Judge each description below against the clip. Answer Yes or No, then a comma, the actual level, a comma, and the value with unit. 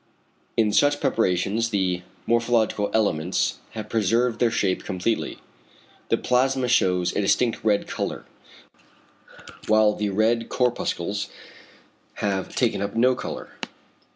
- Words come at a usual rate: No, slow, 115 wpm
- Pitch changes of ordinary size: Yes, average, 3.0 semitones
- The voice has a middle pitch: No, low, 110 Hz